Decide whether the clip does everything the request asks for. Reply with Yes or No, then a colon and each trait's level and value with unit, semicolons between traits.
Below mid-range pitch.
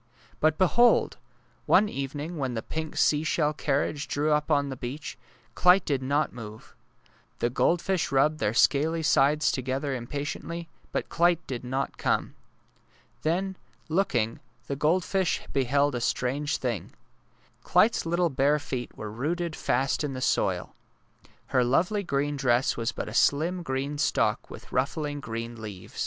No: medium, 145 Hz